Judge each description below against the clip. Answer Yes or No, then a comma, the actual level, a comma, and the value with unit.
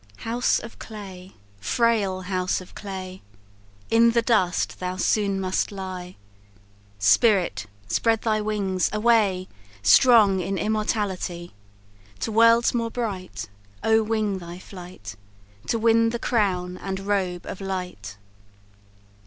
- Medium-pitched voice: No, high, 195 Hz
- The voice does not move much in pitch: No, average, 3.4 semitones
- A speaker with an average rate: No, slow, 120 wpm